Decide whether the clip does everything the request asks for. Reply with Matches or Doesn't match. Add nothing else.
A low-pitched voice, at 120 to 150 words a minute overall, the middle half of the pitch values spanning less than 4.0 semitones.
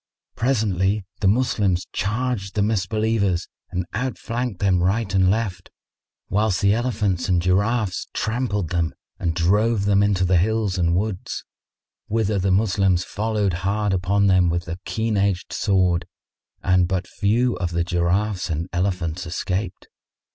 Matches